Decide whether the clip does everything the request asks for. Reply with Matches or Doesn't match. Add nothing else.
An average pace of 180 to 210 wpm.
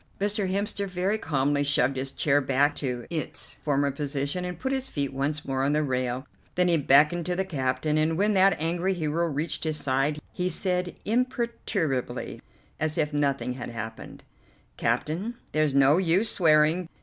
Doesn't match